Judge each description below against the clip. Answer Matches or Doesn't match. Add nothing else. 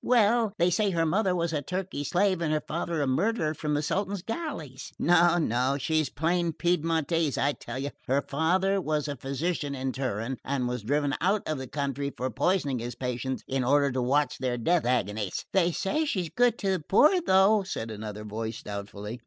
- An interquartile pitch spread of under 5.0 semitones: Doesn't match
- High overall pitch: Doesn't match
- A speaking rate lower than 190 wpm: Doesn't match